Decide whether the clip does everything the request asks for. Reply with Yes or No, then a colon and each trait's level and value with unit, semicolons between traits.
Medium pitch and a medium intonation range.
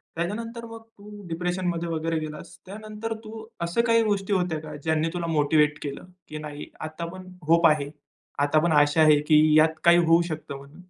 Yes: medium, 165 Hz; average, 4.2 semitones